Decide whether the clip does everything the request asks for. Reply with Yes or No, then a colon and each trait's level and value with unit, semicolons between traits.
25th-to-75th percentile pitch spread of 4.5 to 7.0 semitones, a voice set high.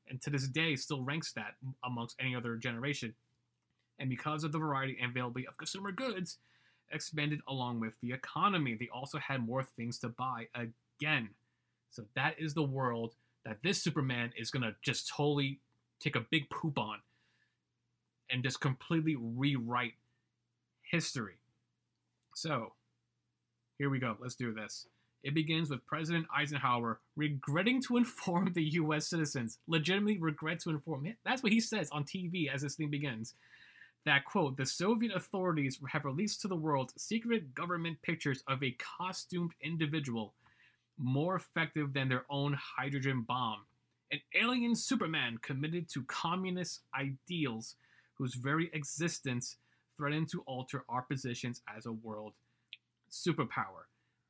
No: average, 4.8 semitones; medium, 140 Hz